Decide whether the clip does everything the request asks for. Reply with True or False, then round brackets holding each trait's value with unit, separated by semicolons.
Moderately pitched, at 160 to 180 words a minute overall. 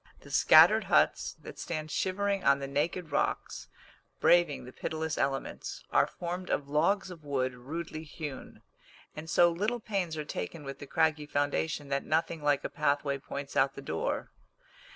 True (155 Hz; 165 wpm)